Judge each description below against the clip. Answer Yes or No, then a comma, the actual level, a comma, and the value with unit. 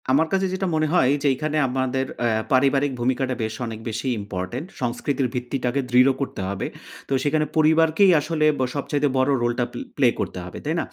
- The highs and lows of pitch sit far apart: No, average, 3.8 semitones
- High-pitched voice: No, low, 135 Hz